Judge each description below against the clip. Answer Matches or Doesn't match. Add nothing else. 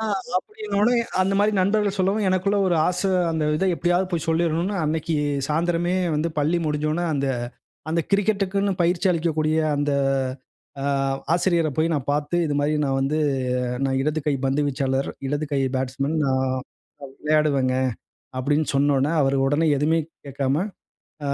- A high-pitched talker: Doesn't match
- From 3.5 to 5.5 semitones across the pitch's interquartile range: Matches